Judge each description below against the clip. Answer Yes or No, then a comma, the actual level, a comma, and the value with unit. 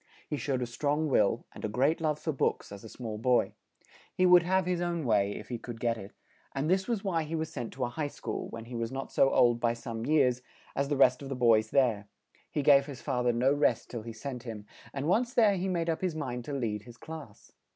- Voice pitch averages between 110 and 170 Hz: Yes, low, 135 Hz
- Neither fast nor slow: No, fast, 255 wpm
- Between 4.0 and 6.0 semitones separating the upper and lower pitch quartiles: Yes, average, 5.1 semitones